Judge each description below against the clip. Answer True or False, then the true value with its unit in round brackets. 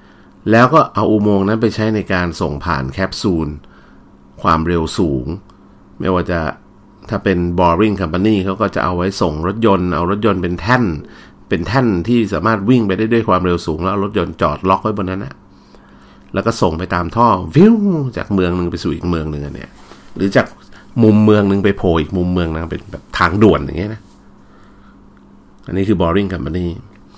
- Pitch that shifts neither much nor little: True (3.8 semitones)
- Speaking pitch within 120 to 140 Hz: False (95 Hz)